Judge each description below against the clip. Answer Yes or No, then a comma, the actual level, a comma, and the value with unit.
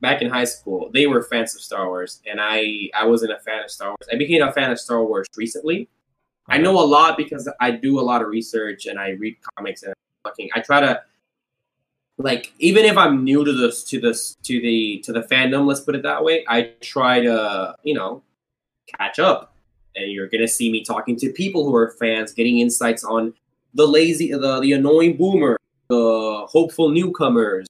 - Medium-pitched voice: No, low, 120 Hz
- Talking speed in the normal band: No, fast, 210 wpm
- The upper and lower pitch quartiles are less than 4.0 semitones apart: No, average, 4.5 semitones